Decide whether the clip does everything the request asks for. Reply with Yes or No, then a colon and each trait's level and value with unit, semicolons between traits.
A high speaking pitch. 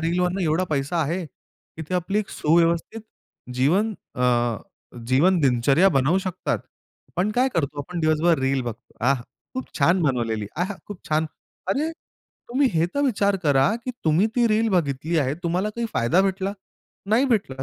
No: medium, 170 Hz